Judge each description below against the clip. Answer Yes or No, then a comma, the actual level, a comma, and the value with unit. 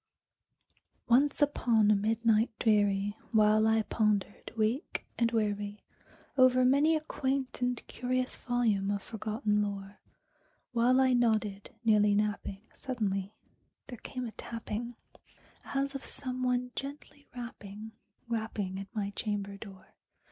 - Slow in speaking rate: Yes, slow, 125 wpm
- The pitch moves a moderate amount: Yes, average, 3.3 semitones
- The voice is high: Yes, high, 220 Hz